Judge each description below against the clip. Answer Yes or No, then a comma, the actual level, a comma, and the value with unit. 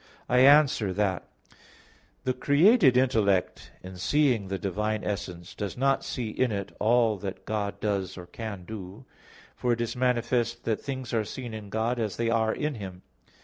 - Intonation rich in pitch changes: No, average, 3.8 semitones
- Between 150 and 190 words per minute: Yes, average, 170 wpm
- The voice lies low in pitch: Yes, low, 110 Hz